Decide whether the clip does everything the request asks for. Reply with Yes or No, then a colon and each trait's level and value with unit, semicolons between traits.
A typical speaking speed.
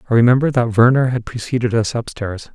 Yes: average, 190 wpm